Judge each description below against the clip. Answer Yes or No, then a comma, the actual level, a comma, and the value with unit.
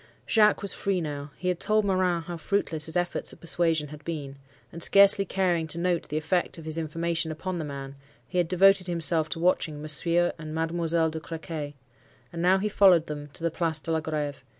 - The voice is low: No, medium, 165 Hz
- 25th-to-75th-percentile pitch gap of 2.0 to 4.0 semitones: Yes, narrow, 2.5 semitones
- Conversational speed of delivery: No, fast, 210 wpm